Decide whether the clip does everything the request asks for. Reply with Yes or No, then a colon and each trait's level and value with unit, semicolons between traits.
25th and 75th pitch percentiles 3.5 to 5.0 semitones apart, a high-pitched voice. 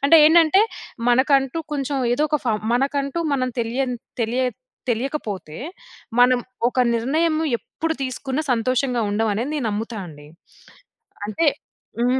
Yes: average, 4.0 semitones; very high, 255 Hz